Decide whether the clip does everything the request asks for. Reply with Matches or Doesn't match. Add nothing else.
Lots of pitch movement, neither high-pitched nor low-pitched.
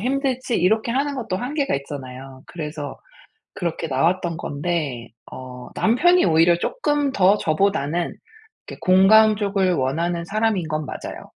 Matches